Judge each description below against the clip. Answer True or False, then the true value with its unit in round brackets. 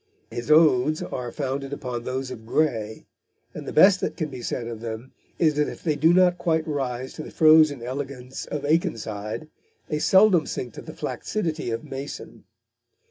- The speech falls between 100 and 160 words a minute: False (180 wpm)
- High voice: False (140 Hz)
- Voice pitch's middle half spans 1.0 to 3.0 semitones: False (4.2 semitones)